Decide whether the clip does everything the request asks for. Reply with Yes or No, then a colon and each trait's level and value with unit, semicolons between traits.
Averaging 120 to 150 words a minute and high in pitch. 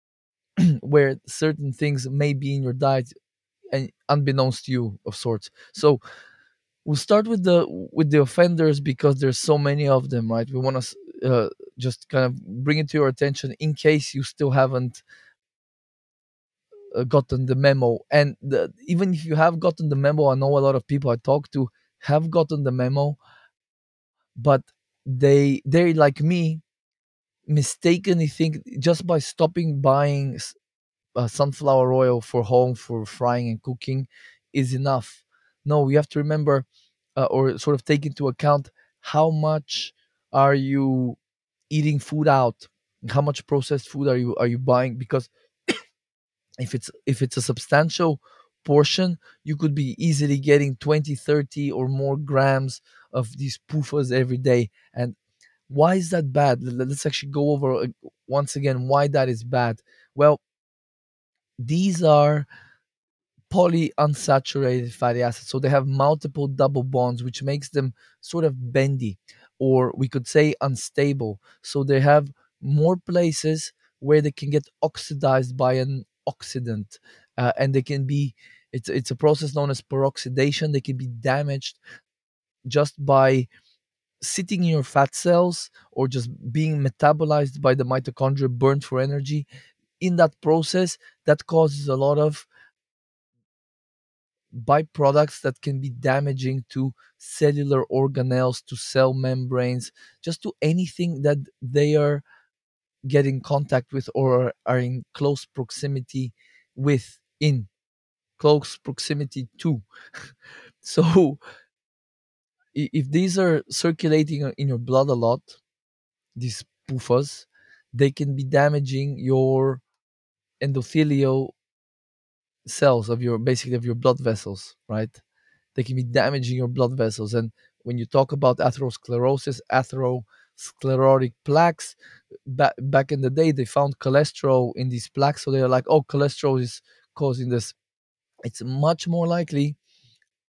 No: average, 140 wpm; medium, 140 Hz